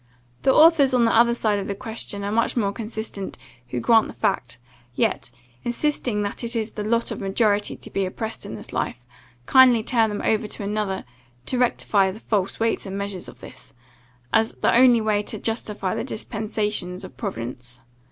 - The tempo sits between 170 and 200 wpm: Yes, average, 190 wpm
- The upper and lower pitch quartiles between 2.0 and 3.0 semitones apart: Yes, average, 2.7 semitones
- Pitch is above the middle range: Yes, high, 215 Hz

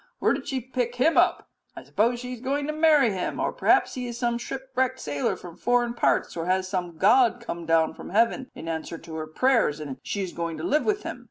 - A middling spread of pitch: No, wide, 7.4 semitones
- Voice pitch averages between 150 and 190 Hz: No, high, 235 Hz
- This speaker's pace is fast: Yes, fast, 240 wpm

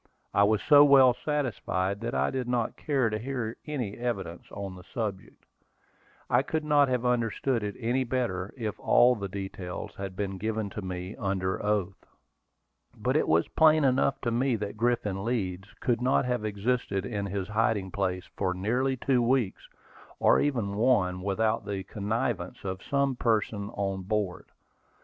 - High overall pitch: No, low, 110 Hz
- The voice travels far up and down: No, average, 4.2 semitones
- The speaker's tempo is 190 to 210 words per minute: No, average, 165 wpm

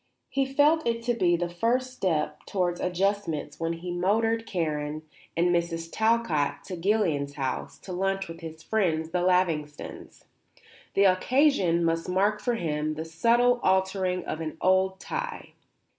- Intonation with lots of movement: No, average, 4.9 semitones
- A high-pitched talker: No, medium, 180 Hz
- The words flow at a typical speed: Yes, average, 150 wpm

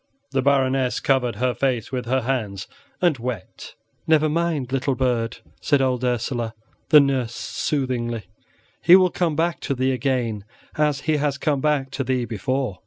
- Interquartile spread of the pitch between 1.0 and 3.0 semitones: Yes, narrow, 2.6 semitones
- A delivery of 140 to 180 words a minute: Yes, average, 165 wpm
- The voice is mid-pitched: No, low, 130 Hz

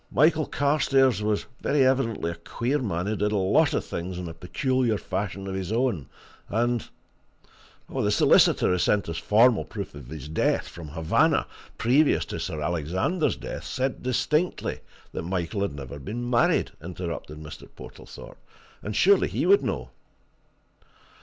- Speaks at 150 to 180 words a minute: Yes, average, 160 wpm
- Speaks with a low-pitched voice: Yes, low, 105 Hz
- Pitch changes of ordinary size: No, wide, 7.0 semitones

